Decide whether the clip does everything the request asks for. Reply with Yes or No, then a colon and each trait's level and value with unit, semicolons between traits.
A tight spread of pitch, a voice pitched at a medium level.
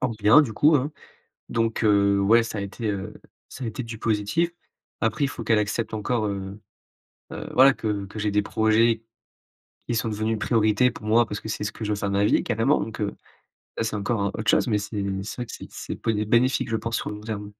No: narrow, 1.9 semitones; low, 110 Hz